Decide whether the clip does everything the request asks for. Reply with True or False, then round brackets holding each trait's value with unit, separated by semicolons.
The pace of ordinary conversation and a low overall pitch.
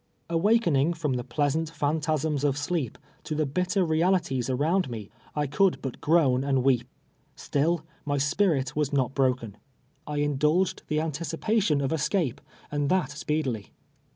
False (150 wpm; 150 Hz)